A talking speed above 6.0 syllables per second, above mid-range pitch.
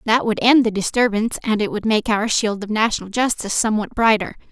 Yes: 6.2 syllables/s; high, 215 Hz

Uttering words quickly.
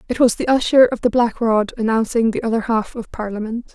Yes: fast, 225 wpm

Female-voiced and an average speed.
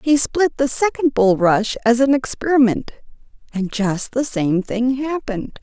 Yes: female; average, 150 wpm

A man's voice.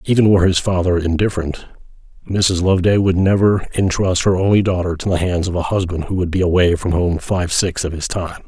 Yes: male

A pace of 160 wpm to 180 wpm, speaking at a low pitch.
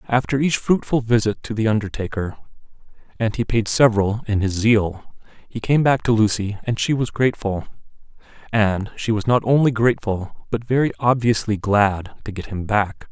Yes: average, 170 wpm; low, 110 Hz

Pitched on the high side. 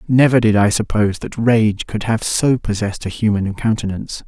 No: low, 110 Hz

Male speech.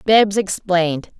No: female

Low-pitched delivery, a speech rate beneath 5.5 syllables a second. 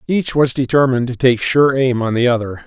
No: low, 125 Hz; 5.6 syllables/s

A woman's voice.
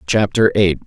No: male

